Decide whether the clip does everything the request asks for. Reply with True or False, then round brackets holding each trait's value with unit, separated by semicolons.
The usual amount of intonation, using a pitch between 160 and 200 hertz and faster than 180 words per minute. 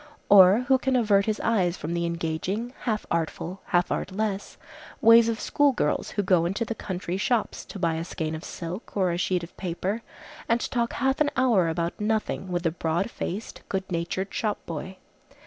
True (4.6 semitones; 190 Hz; 190 wpm)